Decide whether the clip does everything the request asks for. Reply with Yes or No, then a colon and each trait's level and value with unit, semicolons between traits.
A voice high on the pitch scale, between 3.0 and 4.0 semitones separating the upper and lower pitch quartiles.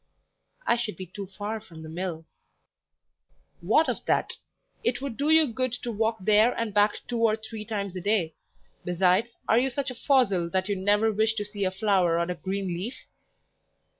Yes: high, 210 Hz; average, 3.6 semitones